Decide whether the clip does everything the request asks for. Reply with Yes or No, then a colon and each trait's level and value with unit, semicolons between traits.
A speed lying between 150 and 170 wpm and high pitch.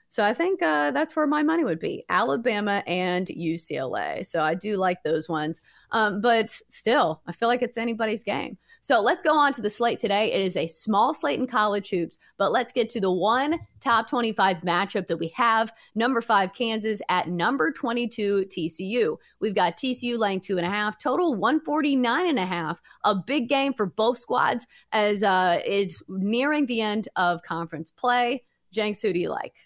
No: average, 195 wpm; high, 215 Hz